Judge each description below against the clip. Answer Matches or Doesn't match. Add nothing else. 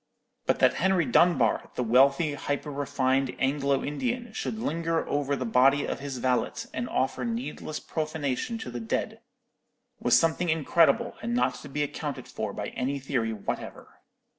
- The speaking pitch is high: Doesn't match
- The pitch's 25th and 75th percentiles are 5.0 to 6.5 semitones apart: Doesn't match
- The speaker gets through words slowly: Doesn't match